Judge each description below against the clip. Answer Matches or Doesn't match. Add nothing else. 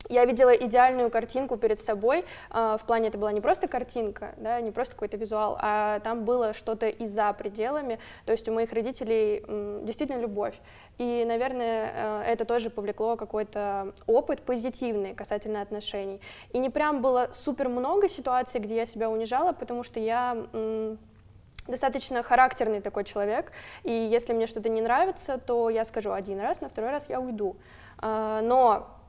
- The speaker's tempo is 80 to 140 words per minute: Doesn't match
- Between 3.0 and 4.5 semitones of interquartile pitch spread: Doesn't match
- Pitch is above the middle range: Matches